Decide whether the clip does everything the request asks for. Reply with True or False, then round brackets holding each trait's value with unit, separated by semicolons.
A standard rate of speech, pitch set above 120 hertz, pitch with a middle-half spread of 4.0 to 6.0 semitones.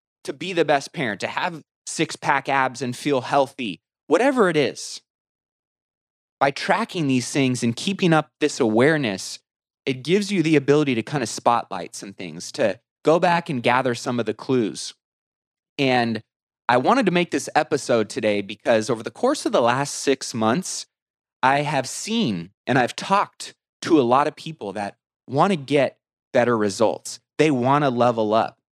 True (175 wpm; 135 Hz; 4.8 semitones)